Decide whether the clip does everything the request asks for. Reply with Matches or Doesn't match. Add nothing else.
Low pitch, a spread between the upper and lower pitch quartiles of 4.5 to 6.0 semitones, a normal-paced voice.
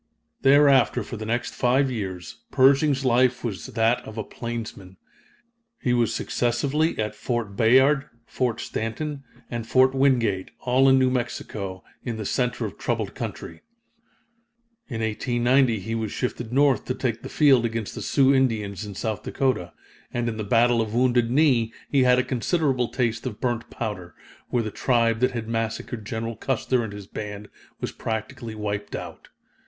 Doesn't match